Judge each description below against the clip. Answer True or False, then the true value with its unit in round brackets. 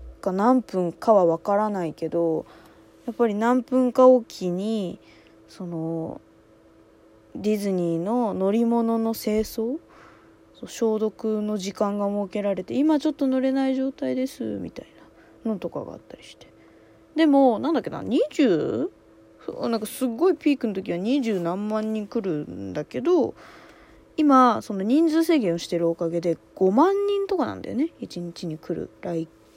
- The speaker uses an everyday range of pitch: False (7.2 semitones)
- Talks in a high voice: True (210 Hz)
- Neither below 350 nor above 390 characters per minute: False (265 characters per minute)